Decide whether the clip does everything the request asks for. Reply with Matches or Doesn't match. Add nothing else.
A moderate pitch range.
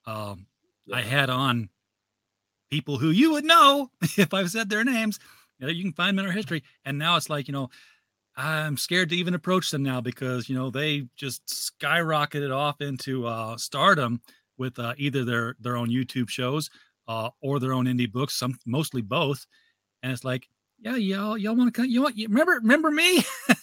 Doesn't match